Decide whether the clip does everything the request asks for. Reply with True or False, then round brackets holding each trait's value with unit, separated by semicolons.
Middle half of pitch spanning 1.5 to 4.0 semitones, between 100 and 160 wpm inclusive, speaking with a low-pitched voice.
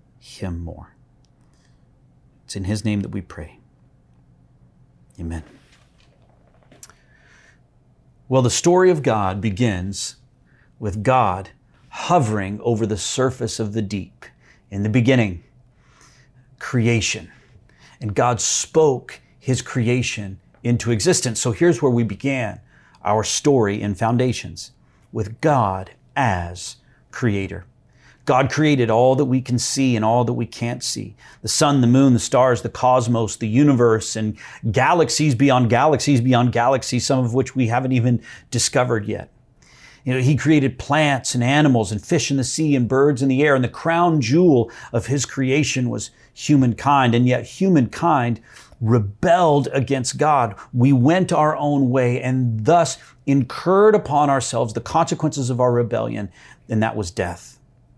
True (3.6 semitones; 140 wpm; 125 Hz)